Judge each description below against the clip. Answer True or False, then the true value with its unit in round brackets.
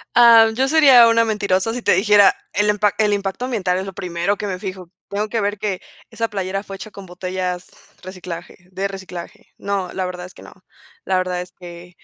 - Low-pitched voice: False (195 Hz)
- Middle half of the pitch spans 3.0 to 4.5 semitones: False (2.5 semitones)